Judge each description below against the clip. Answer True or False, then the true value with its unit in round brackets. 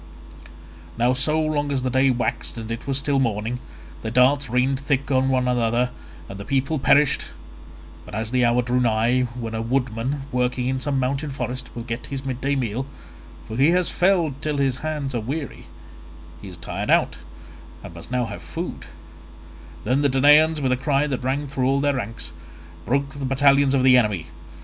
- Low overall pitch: True (130 Hz)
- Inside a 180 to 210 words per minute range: True (185 wpm)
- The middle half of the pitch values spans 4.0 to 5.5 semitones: False (2.9 semitones)